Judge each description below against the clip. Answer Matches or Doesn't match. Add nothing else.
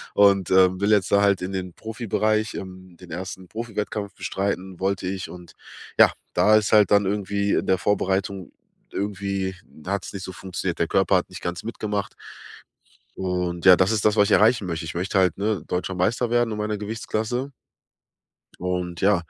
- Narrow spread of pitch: Matches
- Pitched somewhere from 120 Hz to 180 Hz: Doesn't match